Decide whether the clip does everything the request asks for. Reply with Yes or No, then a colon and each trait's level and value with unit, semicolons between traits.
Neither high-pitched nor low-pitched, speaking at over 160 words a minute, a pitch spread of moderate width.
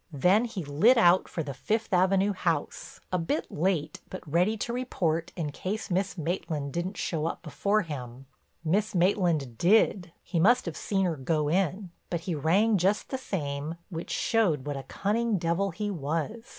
Yes: medium, 175 Hz; average, 170 wpm; average, 4.5 semitones